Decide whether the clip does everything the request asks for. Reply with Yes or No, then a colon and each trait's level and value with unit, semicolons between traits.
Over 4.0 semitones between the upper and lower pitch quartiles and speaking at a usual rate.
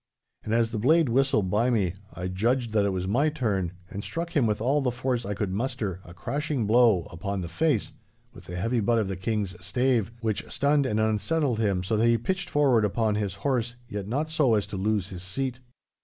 No: average, 4.6 semitones; fast, 220 wpm